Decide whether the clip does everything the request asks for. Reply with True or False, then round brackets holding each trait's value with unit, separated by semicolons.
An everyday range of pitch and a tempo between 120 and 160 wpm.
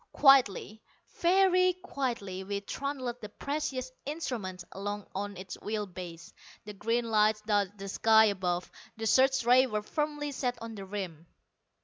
True (5.0 semitones; 145 wpm)